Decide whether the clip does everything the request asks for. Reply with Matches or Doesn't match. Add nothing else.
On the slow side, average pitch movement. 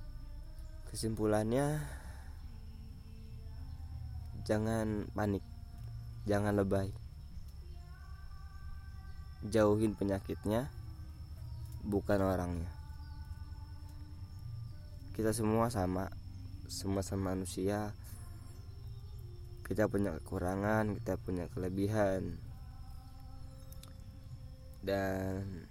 Matches